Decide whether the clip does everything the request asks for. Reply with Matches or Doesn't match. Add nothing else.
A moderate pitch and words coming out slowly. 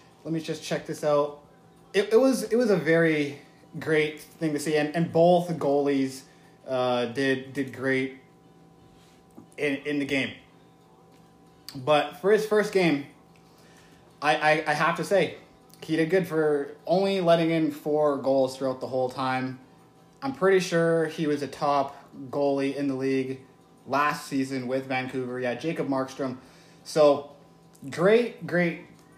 Doesn't match